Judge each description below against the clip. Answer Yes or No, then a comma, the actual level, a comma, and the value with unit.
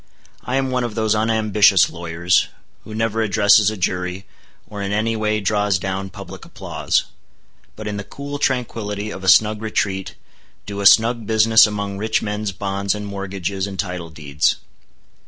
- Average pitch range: No, narrow, 2.2 semitones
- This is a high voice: No, low, 105 Hz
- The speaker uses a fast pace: No, average, 165 wpm